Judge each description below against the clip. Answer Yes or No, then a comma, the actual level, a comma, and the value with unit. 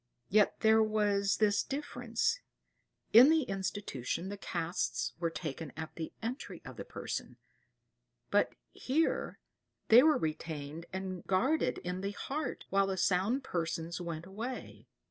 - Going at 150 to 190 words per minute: No, slow, 135 wpm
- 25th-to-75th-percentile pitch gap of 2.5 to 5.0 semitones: No, wide, 5.6 semitones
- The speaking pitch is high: Yes, high, 195 Hz